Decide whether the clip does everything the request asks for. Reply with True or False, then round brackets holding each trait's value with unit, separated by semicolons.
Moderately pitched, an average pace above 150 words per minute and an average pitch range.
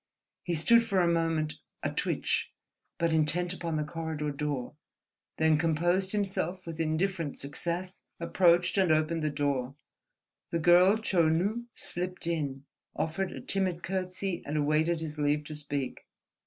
False (165 Hz; 145 wpm; 3.0 semitones)